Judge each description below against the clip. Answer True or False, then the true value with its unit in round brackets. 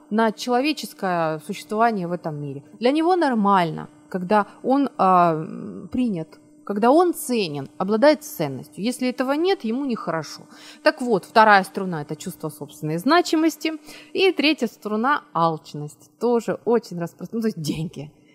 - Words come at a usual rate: True (135 wpm)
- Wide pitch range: True (7.6 semitones)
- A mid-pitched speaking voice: False (210 Hz)